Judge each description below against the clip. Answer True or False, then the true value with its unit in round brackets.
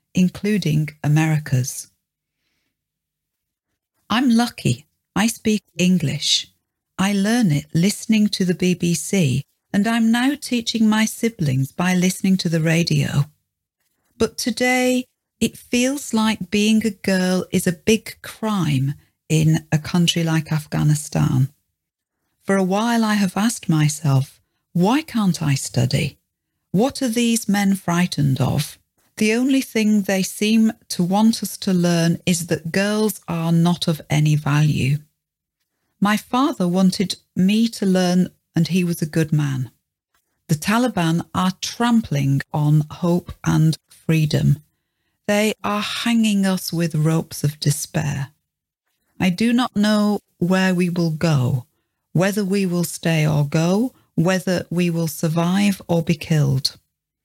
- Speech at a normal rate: False (130 wpm)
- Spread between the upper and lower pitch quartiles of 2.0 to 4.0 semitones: False (5.5 semitones)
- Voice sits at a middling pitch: True (175 Hz)